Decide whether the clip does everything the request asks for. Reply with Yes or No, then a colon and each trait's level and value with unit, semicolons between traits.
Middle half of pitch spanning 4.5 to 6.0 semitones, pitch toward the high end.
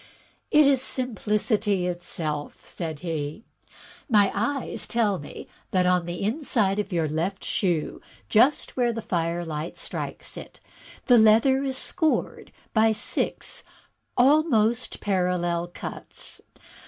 Yes: wide, 5.6 semitones; high, 205 Hz